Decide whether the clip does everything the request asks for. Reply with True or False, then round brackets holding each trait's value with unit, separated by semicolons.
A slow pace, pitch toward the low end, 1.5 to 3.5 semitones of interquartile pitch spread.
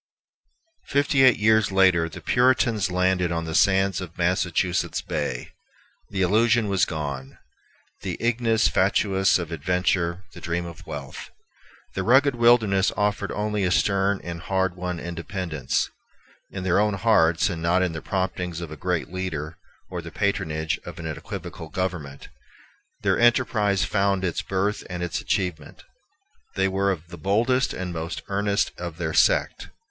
False (155 wpm; 95 Hz; 3.1 semitones)